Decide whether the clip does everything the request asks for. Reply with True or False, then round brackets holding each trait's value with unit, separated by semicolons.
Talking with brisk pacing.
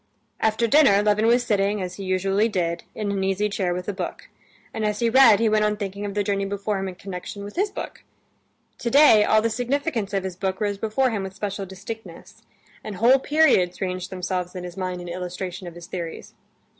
True (215 wpm)